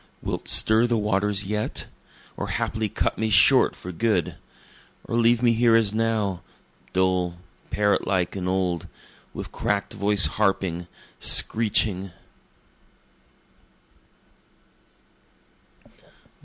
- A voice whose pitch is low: Yes, low, 105 Hz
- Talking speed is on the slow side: Yes, slow, 100 wpm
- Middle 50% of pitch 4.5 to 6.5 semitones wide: No, average, 3.0 semitones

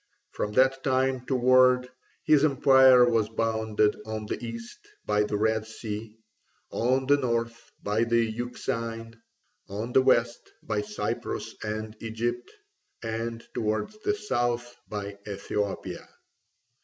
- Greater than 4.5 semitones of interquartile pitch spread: No, average, 2.7 semitones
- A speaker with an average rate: No, slow, 120 wpm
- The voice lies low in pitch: Yes, low, 115 Hz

